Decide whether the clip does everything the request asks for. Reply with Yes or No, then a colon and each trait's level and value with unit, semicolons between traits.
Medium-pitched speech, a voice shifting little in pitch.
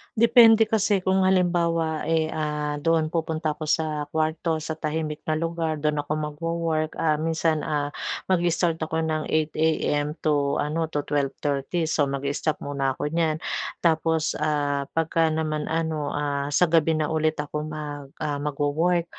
Yes: medium, 155 Hz; narrow, 1.7 semitones